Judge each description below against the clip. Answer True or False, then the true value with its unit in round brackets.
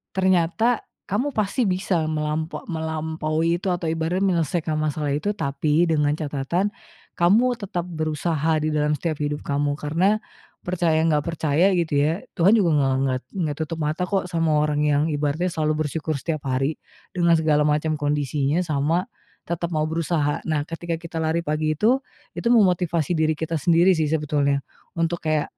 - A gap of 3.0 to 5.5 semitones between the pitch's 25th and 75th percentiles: False (2.5 semitones)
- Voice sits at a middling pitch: True (160 Hz)